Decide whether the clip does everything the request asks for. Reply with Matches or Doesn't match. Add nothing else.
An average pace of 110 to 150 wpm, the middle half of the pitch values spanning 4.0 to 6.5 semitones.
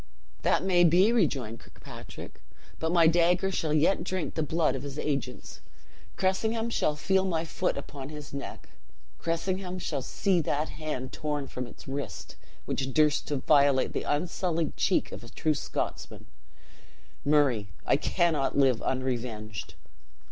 Matches